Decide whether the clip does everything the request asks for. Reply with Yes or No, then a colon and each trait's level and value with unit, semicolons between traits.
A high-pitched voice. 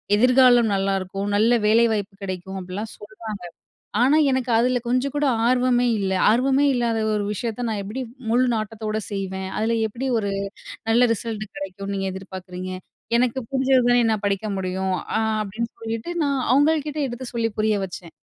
Yes: high, 220 Hz